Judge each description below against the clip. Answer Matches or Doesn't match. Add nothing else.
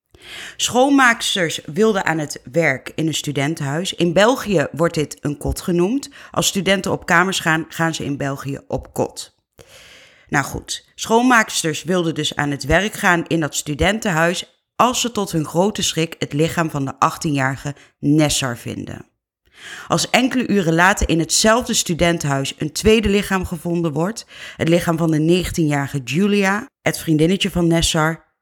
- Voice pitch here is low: Doesn't match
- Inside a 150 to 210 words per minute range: Matches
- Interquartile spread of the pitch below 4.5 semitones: Matches